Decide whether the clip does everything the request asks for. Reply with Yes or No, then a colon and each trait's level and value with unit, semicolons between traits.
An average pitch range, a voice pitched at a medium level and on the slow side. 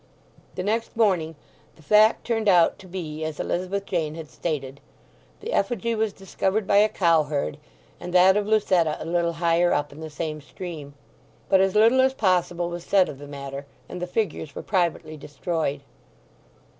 No: average, 4.2 semitones; medium, 175 Hz; average, 175 wpm